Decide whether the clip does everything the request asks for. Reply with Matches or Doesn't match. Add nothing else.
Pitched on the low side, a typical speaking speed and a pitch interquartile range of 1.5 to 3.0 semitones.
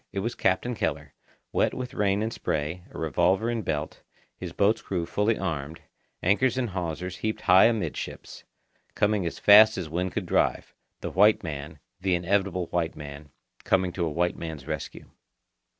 Doesn't match